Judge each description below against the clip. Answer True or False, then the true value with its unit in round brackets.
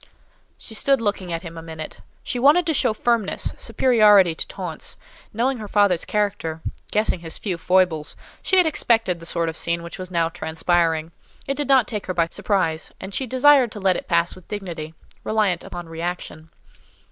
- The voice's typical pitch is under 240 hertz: True (185 Hz)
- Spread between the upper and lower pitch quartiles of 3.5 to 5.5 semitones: True (4.9 semitones)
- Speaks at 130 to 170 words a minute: False (185 wpm)